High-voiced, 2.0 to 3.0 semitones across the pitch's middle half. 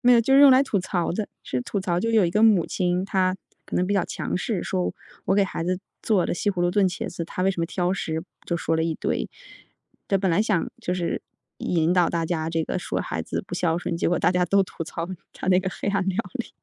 No: medium, 180 Hz; narrow, 2.5 semitones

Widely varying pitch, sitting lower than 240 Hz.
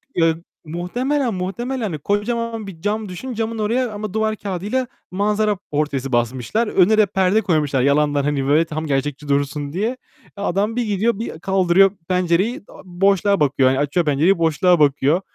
Yes: wide, 6.3 semitones; medium, 185 Hz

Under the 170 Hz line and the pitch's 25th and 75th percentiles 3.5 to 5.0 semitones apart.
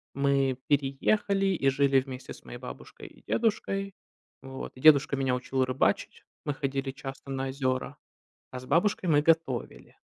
No: low, 135 Hz; average, 2.9 semitones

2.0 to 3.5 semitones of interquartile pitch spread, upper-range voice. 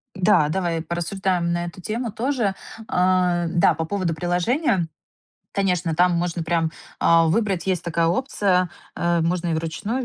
No: narrow, 2.4 semitones; medium, 175 Hz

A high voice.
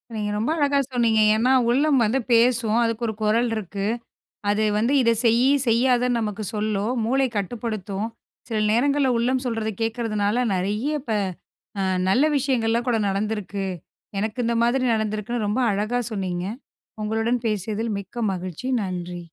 Yes: high, 225 Hz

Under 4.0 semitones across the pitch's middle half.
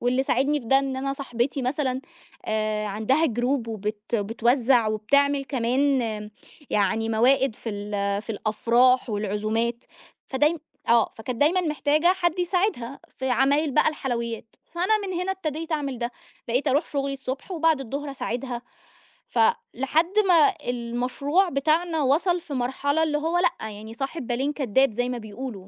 No: average, 4.3 semitones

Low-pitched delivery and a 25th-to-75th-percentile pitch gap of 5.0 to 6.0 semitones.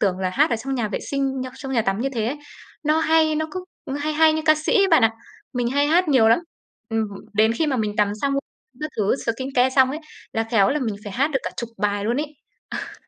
No: very high, 260 Hz; average, 5.3 semitones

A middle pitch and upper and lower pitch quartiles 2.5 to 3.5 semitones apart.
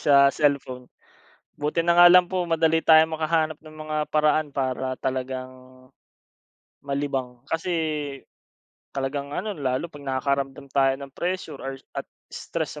Yes: medium, 145 Hz; average, 3.2 semitones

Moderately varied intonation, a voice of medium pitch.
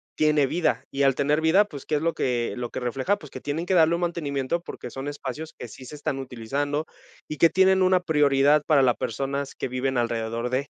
Yes: average, 3.5 semitones; medium, 145 Hz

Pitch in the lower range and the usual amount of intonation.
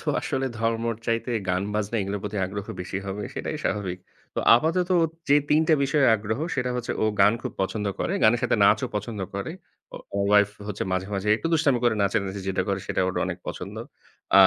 Yes: low, 105 Hz; average, 3.4 semitones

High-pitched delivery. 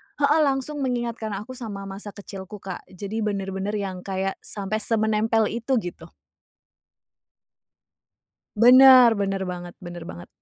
Yes: high, 210 Hz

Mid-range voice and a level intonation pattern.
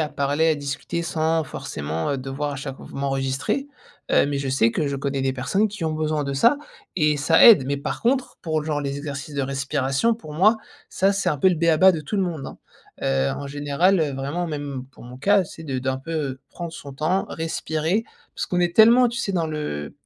No: medium, 150 Hz; average, 3.8 semitones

